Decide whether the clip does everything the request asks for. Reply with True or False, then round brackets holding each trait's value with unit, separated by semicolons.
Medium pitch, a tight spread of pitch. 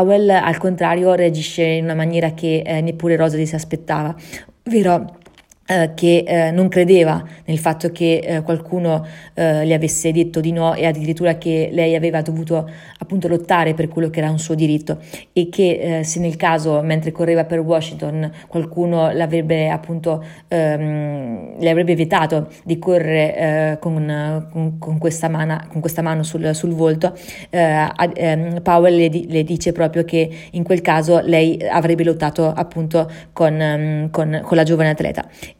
True (165 Hz; 1.2 semitones)